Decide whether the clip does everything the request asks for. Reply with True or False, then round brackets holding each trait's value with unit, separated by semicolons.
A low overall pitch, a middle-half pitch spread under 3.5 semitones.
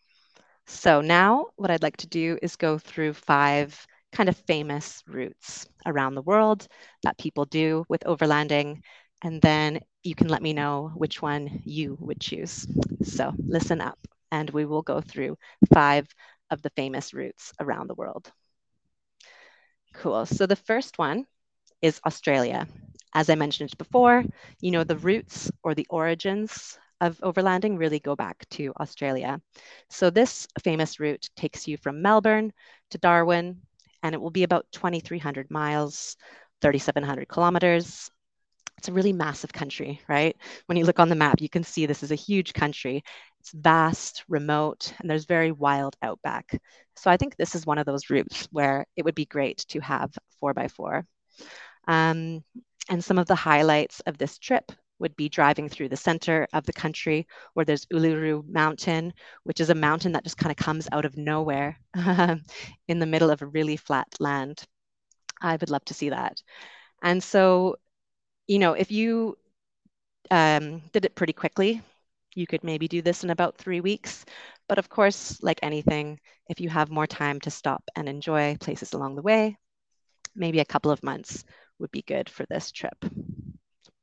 False (160 Hz; 3.0 semitones)